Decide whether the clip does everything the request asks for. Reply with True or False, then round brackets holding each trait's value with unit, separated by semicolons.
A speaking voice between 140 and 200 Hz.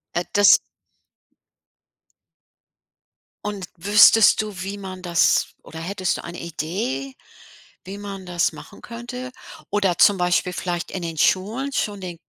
True (190 Hz)